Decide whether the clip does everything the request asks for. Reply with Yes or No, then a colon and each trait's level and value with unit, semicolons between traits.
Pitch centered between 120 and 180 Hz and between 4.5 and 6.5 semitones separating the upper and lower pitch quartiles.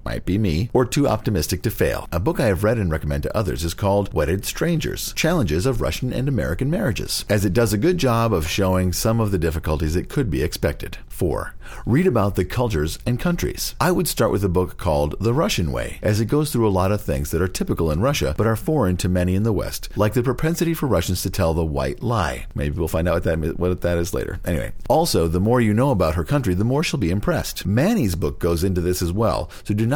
No: low, 100 Hz; average, 5.0 semitones